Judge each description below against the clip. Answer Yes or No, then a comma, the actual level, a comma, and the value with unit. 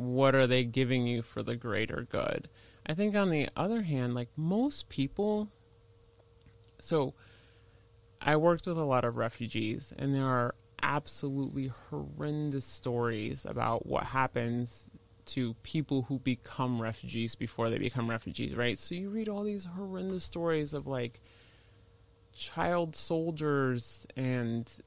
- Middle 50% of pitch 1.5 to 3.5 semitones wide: No, average, 4.4 semitones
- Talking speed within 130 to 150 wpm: Yes, average, 140 wpm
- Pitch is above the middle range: No, low, 125 Hz